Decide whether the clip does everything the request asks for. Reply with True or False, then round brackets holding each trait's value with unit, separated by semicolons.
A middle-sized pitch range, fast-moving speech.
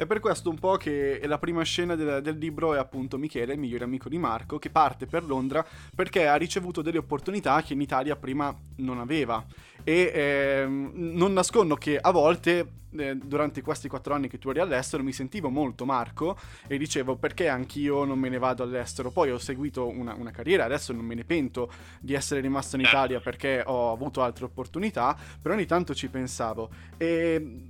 True (3.7 semitones; 195 wpm)